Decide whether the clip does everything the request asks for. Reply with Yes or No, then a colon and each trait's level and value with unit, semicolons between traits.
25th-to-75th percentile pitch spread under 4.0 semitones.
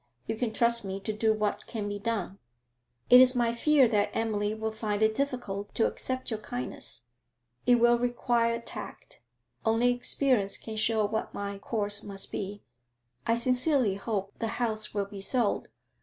Yes: average, 2.8 semitones